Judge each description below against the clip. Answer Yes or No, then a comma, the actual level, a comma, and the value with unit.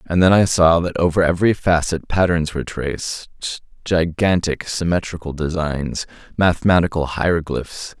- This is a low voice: Yes, very low, 85 Hz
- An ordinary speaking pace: No, slow, 120 wpm